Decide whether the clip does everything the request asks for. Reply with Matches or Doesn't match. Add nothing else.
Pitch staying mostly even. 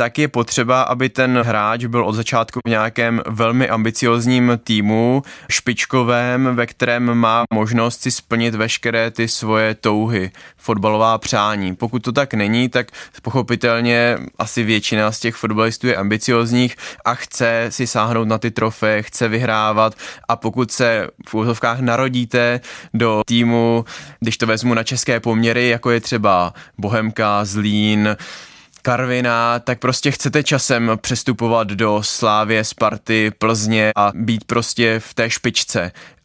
Matches